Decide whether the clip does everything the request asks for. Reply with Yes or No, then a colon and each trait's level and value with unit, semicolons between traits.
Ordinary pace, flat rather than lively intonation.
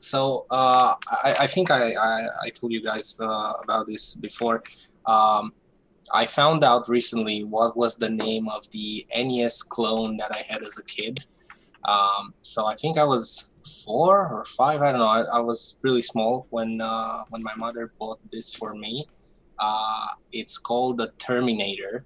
Yes: average, 175 wpm; narrow, 1.9 semitones